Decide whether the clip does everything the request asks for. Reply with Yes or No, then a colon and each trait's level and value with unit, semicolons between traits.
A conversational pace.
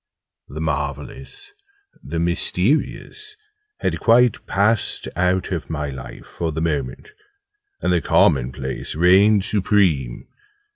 No: slow, 110 wpm